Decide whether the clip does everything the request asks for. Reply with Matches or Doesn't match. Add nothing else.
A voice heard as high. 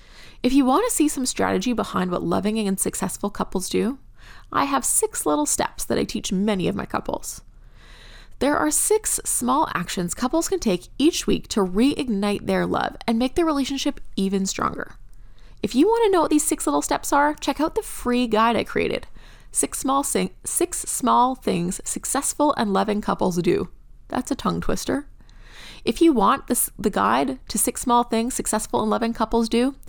Matches